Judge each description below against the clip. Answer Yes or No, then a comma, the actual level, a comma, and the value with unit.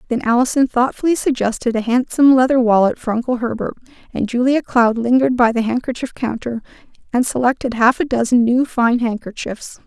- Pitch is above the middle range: Yes, high, 240 Hz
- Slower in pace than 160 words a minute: No, average, 165 wpm